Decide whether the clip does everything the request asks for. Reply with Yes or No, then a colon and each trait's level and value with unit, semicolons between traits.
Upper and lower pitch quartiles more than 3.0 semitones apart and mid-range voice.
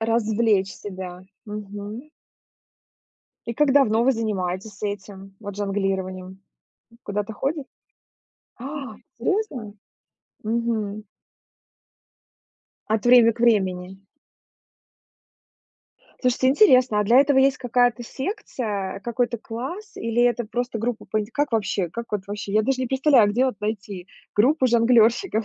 No: average, 3.6 semitones; high, 225 Hz